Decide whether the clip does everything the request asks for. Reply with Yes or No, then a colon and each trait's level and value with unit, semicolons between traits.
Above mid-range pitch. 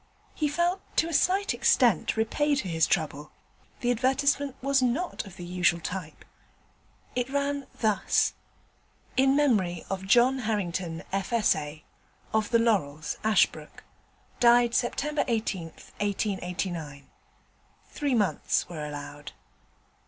Yes: high, 220 Hz